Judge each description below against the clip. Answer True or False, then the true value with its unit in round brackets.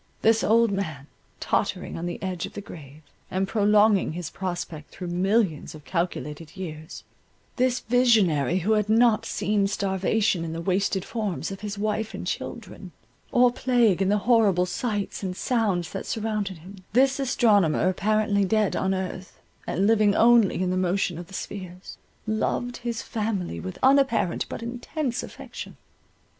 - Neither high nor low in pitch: False (200 Hz)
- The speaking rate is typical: True (150 wpm)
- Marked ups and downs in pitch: False (3.7 semitones)